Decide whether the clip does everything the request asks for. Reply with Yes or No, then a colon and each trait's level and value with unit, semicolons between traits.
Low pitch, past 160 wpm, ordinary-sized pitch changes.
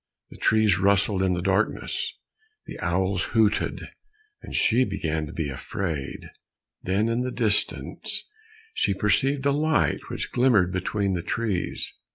No: low, 100 Hz; average, 140 wpm; average, 4.0 semitones